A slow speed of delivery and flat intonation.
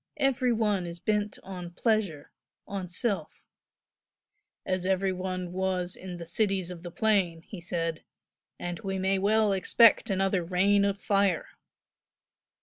No: average, 145 wpm; narrow, 2.3 semitones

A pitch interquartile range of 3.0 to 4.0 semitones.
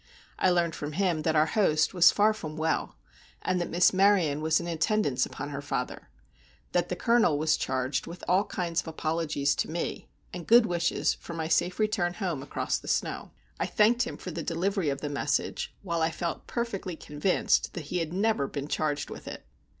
Yes: average, 3.5 semitones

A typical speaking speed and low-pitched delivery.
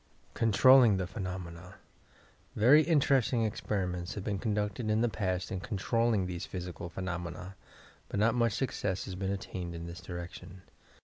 Yes: average, 150 wpm; very low, 95 Hz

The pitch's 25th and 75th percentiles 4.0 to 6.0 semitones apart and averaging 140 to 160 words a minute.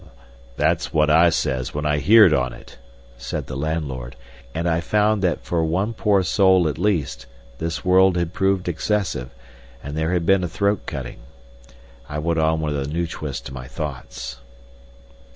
No: average, 4.3 semitones; average, 170 wpm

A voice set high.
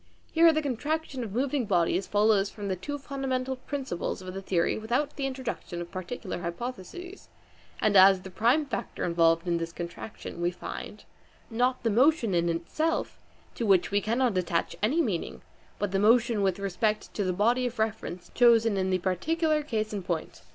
Yes: high, 215 Hz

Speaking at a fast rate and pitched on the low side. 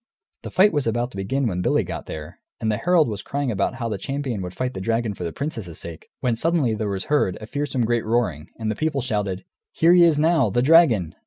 Yes: fast, 245 wpm; low, 120 Hz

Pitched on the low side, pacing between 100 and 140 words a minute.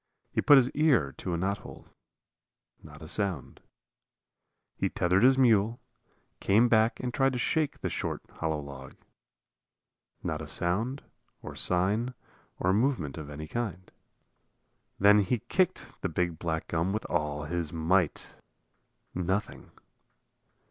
Yes: very low, 95 Hz; slow, 135 wpm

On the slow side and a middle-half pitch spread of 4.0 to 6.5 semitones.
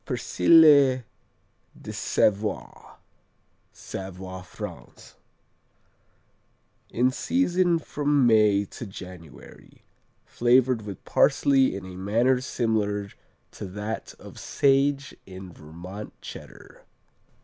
Yes: slow, 85 wpm; wide, 5.6 semitones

